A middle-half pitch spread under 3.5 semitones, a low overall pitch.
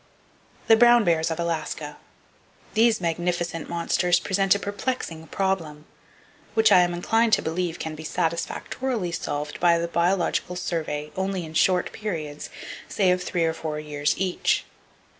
No: average, 3.0 semitones; medium, 175 Hz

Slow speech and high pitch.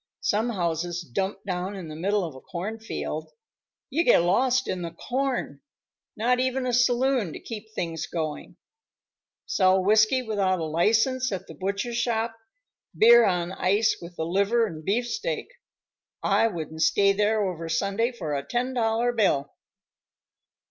No: average, 150 wpm; high, 200 Hz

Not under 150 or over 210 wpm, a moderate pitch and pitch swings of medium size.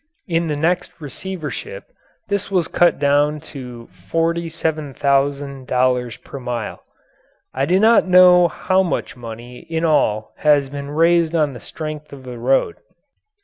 No: slow, 135 wpm; medium, 150 Hz; average, 4.2 semitones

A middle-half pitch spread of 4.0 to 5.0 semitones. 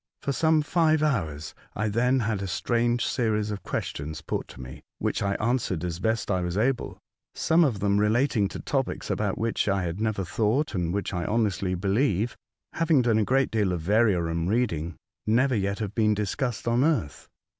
Yes: average, 4.7 semitones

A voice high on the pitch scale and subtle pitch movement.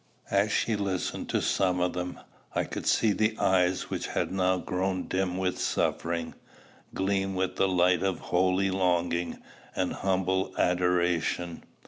No: very low, 95 Hz; narrow, 1.3 semitones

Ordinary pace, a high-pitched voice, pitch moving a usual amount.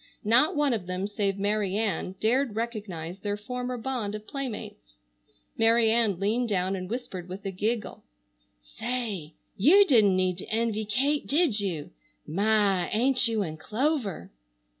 Yes: average, 150 wpm; high, 215 Hz; average, 4.1 semitones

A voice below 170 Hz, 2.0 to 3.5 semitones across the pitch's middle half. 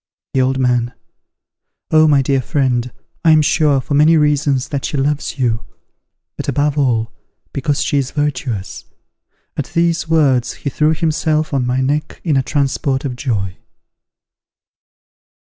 Yes: medium, 140 Hz; average, 2.8 semitones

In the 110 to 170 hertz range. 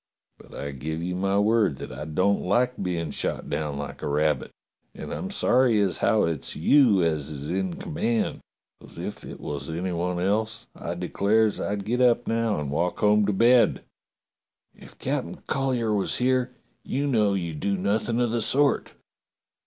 No: low, 100 Hz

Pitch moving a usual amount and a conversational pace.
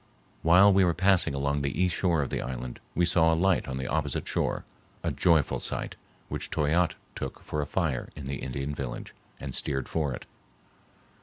Yes: average, 4.1 semitones; average, 190 wpm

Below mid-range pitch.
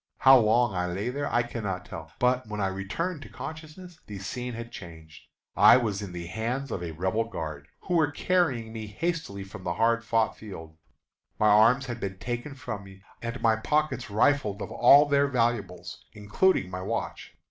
Yes: low, 115 Hz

